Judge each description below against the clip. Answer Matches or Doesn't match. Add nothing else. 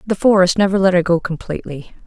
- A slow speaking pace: Doesn't match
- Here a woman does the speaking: Matches